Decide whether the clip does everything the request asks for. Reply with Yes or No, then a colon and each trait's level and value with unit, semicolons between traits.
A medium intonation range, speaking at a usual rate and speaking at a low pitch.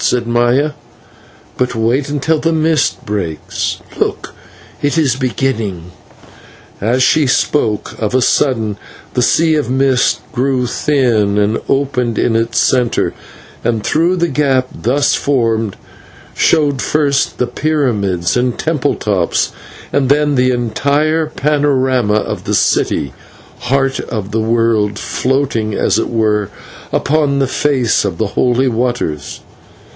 No: average, 4.1 semitones; slow, 130 wpm; low, 125 Hz